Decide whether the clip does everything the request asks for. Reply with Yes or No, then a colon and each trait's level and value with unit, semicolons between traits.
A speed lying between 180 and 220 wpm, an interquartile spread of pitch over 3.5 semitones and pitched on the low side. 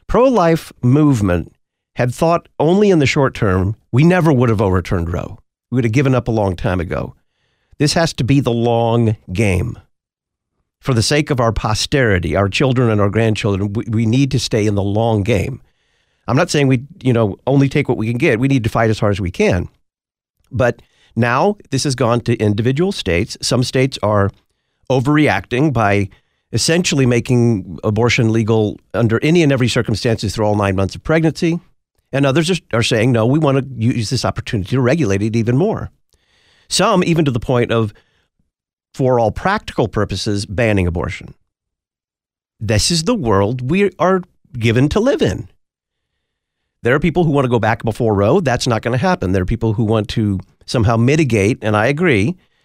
Yes: average, 185 wpm; average, 4.6 semitones; low, 115 Hz